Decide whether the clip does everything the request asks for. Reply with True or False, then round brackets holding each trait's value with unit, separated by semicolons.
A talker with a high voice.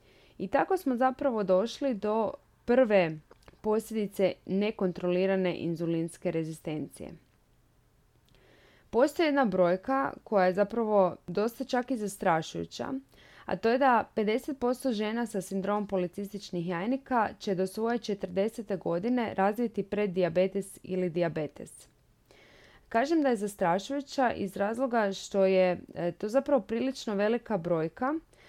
True (205 Hz)